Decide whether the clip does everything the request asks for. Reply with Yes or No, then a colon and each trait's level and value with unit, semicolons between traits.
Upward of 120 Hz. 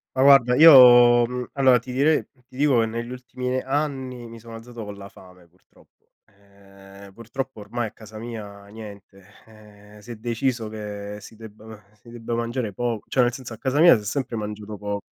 No: low, 115 Hz